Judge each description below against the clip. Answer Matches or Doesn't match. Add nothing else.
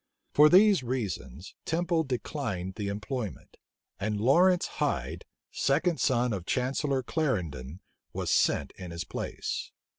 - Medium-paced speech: Doesn't match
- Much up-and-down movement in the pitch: Matches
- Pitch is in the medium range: Doesn't match